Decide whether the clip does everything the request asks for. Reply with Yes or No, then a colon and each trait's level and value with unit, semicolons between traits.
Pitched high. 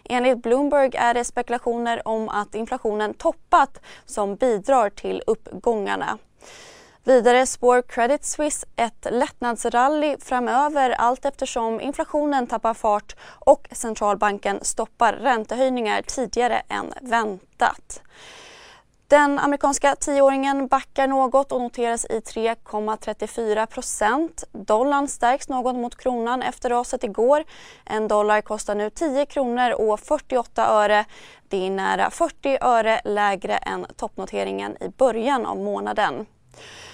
Yes: high, 245 Hz